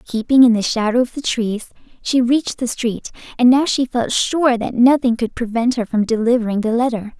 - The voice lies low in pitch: No, high, 240 Hz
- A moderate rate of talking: No, fast, 210 wpm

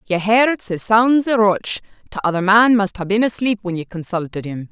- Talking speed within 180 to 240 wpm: Yes, fast, 205 wpm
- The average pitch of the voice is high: Yes, high, 205 Hz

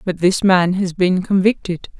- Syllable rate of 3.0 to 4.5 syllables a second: Yes, 4.4 syllables/s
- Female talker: Yes, female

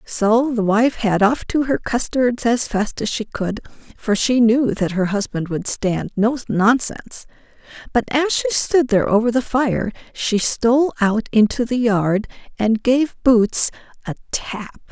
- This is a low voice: No, high, 230 Hz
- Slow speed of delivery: No, average, 170 wpm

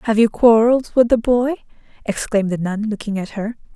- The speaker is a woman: Yes, female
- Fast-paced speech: No, average, 190 wpm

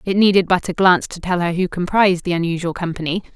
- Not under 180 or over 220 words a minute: No, fast, 230 wpm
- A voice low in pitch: No, medium, 180 Hz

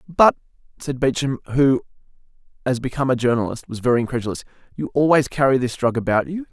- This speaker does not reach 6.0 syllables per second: No, 6.5 syllables/s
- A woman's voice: No, male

